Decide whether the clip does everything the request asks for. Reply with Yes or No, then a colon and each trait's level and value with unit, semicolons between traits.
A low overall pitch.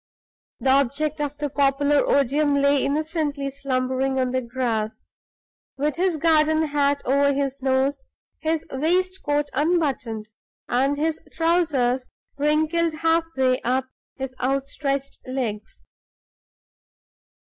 No: very high, 280 Hz